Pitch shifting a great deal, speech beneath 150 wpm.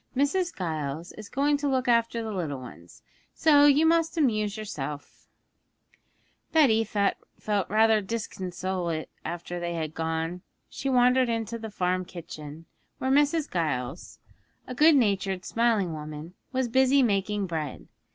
Yes: wide, 7.1 semitones; slow, 135 wpm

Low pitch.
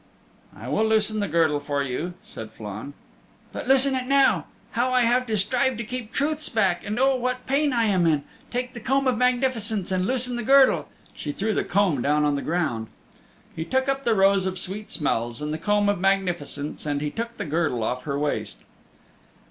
No: high, 205 Hz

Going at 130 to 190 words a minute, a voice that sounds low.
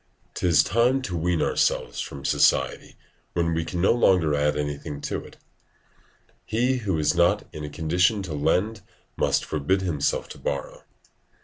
Yes: average, 155 wpm; very low, 85 Hz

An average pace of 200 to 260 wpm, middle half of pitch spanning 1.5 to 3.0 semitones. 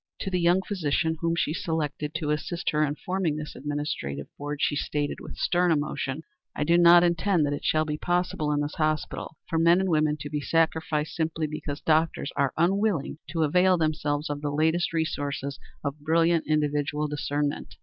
No: average, 185 wpm; narrow, 2.4 semitones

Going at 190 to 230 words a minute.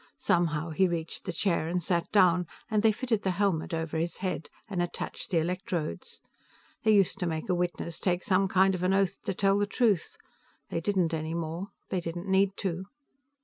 Yes: average, 195 wpm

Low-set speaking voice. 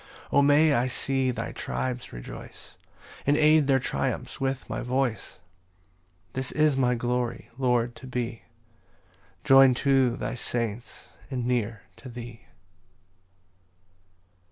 Yes: low, 125 Hz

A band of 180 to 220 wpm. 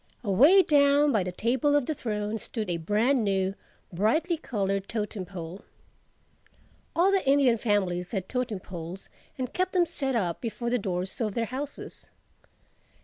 No: average, 155 wpm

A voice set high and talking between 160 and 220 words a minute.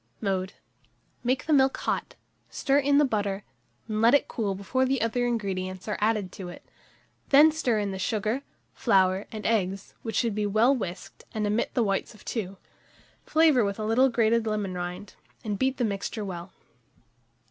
Yes: high, 215 Hz; average, 180 wpm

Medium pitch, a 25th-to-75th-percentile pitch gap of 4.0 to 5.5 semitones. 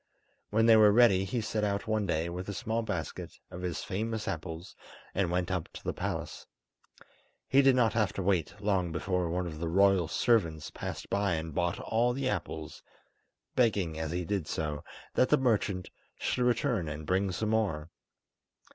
No: very low, 95 Hz; average, 4.6 semitones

